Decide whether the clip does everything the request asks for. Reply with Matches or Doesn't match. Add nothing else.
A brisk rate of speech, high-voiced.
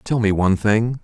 Doesn't match